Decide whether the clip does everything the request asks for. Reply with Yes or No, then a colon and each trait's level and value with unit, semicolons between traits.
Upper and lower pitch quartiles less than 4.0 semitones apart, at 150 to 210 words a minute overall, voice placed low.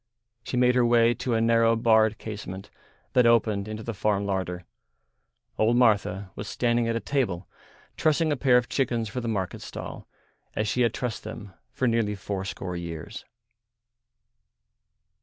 Yes: average, 3.0 semitones; average, 160 wpm; low, 115 Hz